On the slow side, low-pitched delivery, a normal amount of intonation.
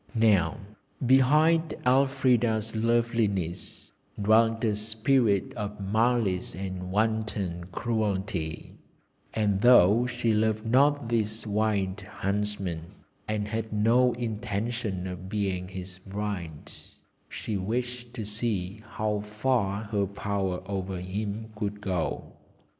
Yes: slow, 105 wpm; low, 105 Hz; average, 3.0 semitones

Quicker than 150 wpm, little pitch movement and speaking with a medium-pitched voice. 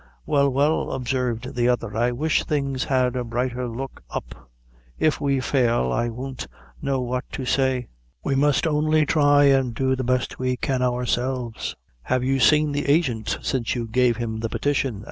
No: average, 175 wpm; narrow, 2.3 semitones; low, 130 Hz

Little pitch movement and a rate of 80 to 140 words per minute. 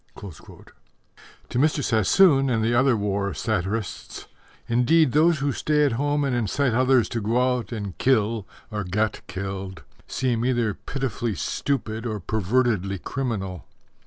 No: average, 4.4 semitones; slow, 135 wpm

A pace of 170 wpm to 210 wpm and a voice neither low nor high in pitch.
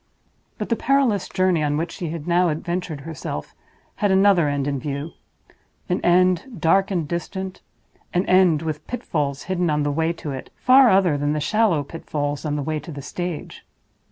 Yes: average, 175 wpm; medium, 165 Hz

